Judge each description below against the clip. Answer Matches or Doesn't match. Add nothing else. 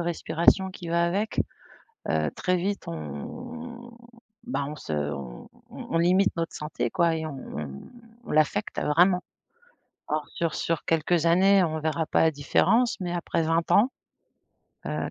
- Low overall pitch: Doesn't match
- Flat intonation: Doesn't match